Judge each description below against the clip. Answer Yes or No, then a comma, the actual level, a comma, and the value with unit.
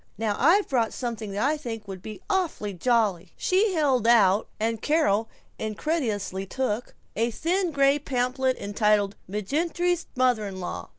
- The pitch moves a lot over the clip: Yes, wide, 5.9 semitones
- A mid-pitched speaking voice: No, high, 235 Hz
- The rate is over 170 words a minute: No, average, 145 wpm